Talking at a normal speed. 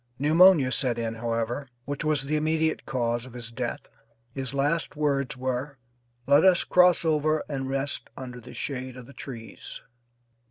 Yes: average, 160 wpm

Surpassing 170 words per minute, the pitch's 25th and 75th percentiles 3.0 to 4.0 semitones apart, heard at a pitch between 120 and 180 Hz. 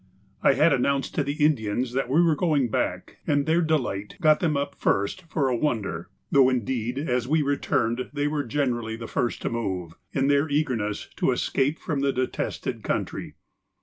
Yes: average, 180 wpm; average, 3.7 semitones; low, 135 Hz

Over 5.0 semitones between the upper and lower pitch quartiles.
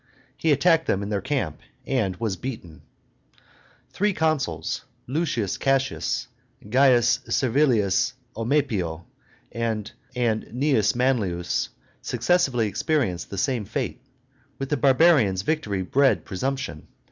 Yes: wide, 5.4 semitones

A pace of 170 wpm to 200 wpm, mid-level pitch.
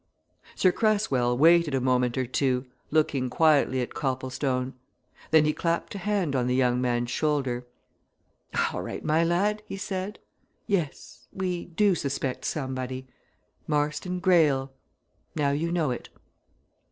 No: slow, 135 wpm; medium, 145 Hz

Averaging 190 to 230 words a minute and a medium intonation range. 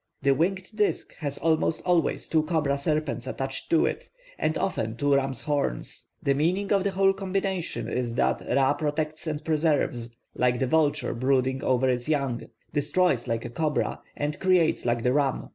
No: average, 175 wpm; average, 3.8 semitones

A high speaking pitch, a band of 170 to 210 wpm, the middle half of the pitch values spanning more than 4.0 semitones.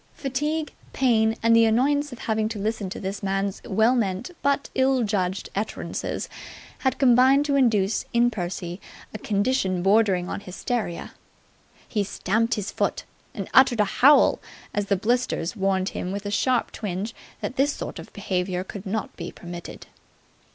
No: high, 215 Hz; average, 160 wpm; average, 4.5 semitones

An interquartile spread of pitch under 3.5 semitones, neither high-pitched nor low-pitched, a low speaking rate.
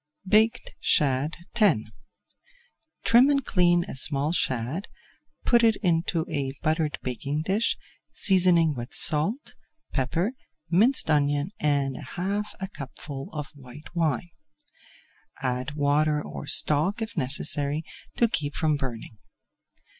No: average, 5.0 semitones; medium, 155 Hz; slow, 115 wpm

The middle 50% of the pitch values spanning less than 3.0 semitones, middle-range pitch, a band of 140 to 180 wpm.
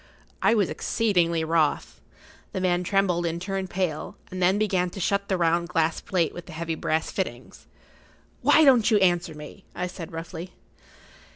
Yes: narrow, 2.6 semitones; medium, 175 Hz; average, 175 wpm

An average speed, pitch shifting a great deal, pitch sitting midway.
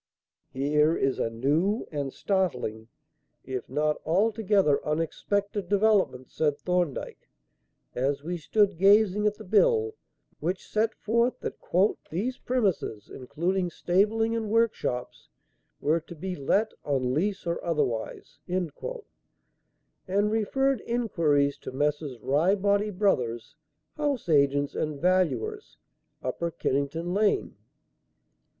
No: slow, 110 wpm; wide, 6.4 semitones; medium, 180 Hz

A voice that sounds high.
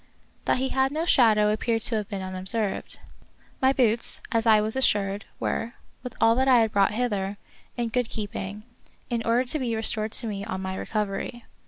Yes: high, 225 Hz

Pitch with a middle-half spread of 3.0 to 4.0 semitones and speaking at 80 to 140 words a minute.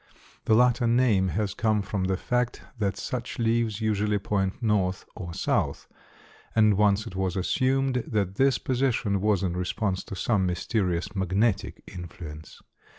No: average, 3.5 semitones; average, 150 wpm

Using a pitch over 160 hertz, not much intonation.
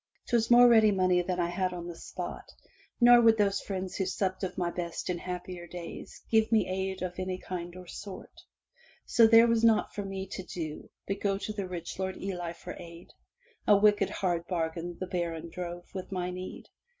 Yes: medium, 185 Hz; narrow, 2.3 semitones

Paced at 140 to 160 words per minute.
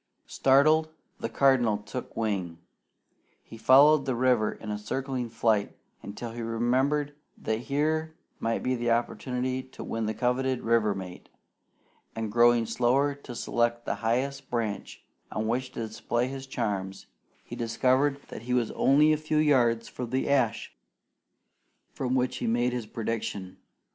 Yes: average, 155 wpm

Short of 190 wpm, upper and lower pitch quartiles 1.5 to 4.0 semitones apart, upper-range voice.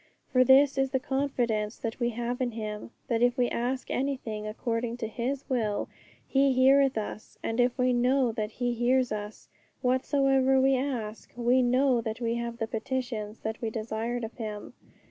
Yes: average, 180 wpm; narrow, 2.6 semitones; high, 245 Hz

